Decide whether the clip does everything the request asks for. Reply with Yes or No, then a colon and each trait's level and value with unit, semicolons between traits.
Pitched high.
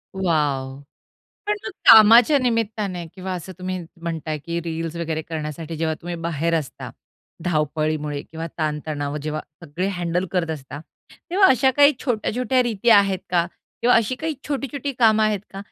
No: medium, 175 Hz